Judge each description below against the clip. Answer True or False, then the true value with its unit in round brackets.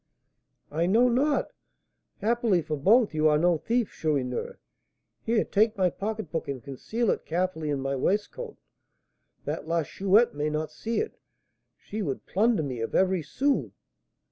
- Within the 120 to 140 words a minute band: False (150 wpm)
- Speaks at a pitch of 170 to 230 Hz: True (185 Hz)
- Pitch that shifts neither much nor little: False (6.7 semitones)